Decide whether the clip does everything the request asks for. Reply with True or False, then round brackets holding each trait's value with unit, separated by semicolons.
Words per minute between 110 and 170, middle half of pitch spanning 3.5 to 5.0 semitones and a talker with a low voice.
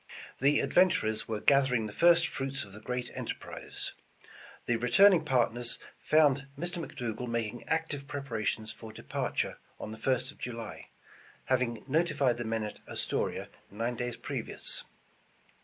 True (145 wpm; 4.0 semitones; 125 Hz)